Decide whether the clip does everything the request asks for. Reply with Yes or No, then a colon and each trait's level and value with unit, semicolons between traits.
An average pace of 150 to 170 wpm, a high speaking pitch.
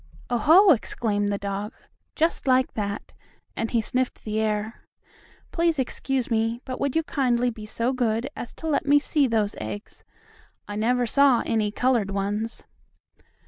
Yes: average, 160 wpm; high, 230 Hz